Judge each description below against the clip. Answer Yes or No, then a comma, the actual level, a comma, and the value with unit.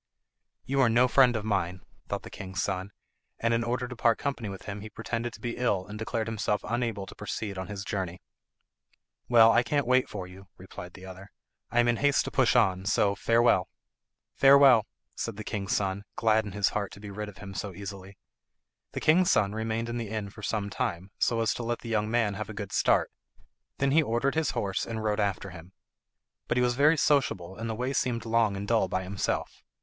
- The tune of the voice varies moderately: Yes, average, 3.2 semitones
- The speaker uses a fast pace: Yes, fast, 220 wpm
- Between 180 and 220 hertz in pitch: No, low, 110 Hz